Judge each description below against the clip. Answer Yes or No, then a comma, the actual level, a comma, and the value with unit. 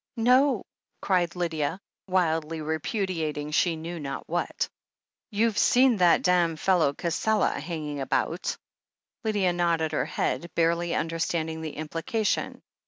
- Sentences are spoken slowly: Yes, slow, 120 wpm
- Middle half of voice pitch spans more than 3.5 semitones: No, average, 2.9 semitones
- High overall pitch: No, medium, 170 Hz